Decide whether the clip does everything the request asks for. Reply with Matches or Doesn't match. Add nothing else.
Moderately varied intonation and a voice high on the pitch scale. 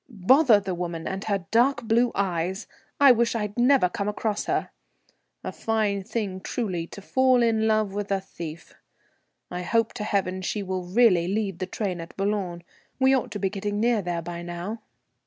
Matches